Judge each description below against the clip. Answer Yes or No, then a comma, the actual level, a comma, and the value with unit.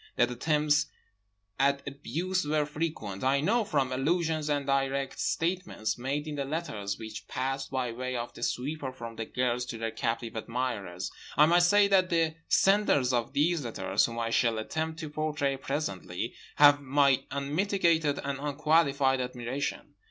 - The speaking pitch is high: No, medium, 140 Hz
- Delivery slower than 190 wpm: Yes, average, 160 wpm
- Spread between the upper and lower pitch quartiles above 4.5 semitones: No, average, 4.0 semitones